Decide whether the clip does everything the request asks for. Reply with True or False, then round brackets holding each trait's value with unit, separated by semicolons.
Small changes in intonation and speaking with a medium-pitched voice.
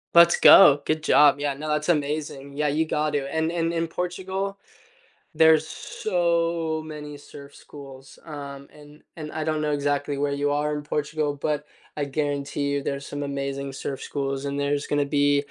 True (1.8 semitones; 145 Hz)